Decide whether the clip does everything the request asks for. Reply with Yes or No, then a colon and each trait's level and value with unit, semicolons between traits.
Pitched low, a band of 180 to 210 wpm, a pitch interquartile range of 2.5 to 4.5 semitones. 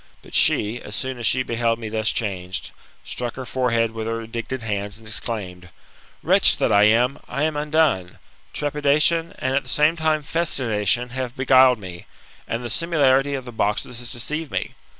Yes: low, 120 Hz; average, 185 wpm; average, 4.1 semitones